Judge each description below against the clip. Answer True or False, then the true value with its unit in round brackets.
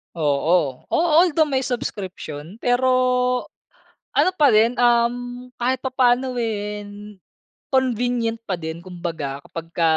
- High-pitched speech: True (235 Hz)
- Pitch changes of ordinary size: False (6.5 semitones)